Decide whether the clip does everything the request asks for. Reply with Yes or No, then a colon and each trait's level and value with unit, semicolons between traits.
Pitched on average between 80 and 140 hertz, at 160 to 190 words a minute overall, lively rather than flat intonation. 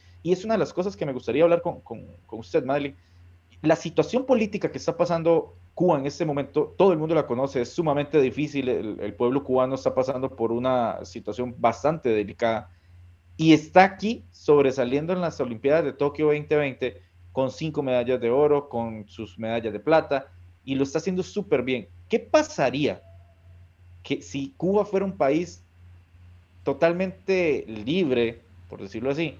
Yes: low, 135 Hz; average, 170 wpm; wide, 7.4 semitones